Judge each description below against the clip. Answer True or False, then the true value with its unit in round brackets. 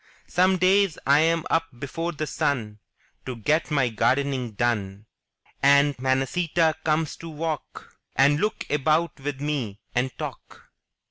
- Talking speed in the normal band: False (130 wpm)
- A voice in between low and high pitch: True (145 Hz)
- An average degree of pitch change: True (4.1 semitones)